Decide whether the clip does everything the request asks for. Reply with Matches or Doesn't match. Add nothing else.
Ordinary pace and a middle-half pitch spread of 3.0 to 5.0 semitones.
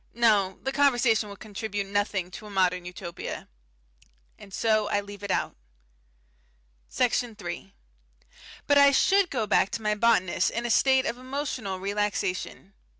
Matches